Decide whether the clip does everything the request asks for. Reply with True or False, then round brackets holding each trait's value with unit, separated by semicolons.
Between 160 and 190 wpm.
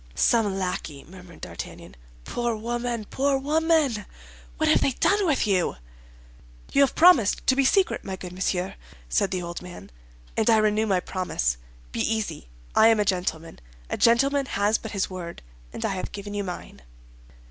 True (170 wpm)